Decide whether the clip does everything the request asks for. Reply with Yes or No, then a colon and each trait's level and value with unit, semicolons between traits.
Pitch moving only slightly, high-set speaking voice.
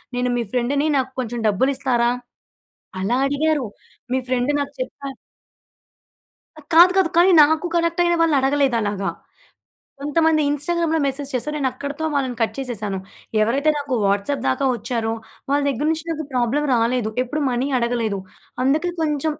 No: average, 4.0 semitones; very high, 275 Hz